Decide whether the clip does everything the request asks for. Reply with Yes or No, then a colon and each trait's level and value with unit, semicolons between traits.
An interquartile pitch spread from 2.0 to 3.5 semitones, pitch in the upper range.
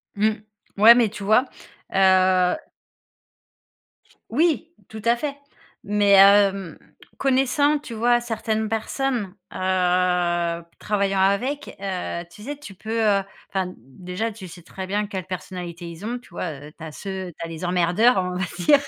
No: average, 4.0 semitones; high, 195 Hz